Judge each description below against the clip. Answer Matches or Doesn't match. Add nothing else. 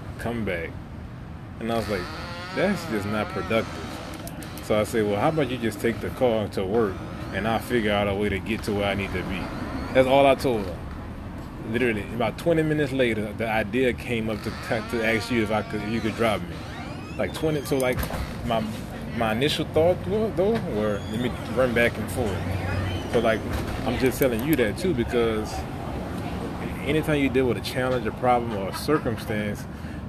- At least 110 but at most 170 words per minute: Doesn't match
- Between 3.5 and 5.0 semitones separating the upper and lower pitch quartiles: Matches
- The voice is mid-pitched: Doesn't match